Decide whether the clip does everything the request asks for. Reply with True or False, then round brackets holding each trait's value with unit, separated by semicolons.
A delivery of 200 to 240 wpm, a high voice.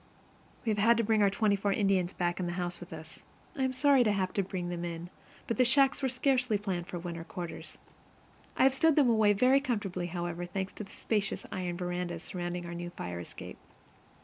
True (205 wpm; 195 Hz)